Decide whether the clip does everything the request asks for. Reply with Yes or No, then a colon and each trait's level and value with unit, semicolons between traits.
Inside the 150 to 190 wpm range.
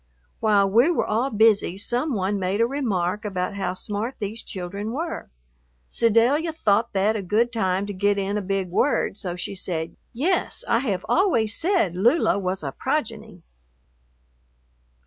Yes: average, 160 wpm